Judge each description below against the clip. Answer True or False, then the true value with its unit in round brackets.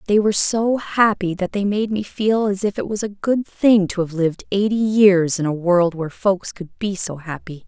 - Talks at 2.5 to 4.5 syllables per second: False (4.9 syllables/s)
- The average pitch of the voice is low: False (195 Hz)